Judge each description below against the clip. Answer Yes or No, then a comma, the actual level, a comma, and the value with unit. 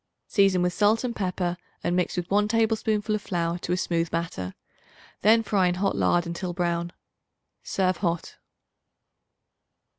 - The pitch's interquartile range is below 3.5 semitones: Yes, average, 3.1 semitones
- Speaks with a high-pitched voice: No, medium, 180 Hz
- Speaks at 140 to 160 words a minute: Yes, average, 150 wpm